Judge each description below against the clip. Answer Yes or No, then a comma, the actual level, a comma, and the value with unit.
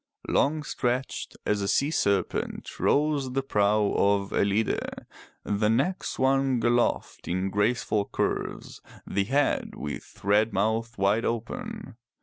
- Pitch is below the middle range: Yes, low, 110 Hz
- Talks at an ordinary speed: No, slow, 125 wpm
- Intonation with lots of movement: No, average, 4.7 semitones